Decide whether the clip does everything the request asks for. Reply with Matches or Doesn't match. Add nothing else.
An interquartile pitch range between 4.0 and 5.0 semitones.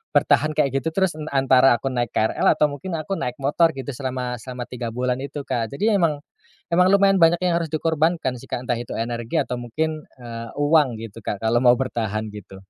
Matches